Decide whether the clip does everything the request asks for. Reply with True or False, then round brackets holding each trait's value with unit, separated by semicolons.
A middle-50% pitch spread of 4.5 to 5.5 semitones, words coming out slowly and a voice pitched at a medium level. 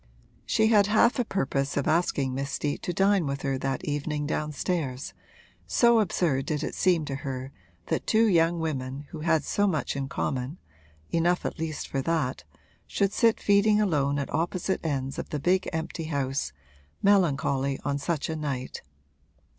False (4.8 semitones; 170 wpm; 155 Hz)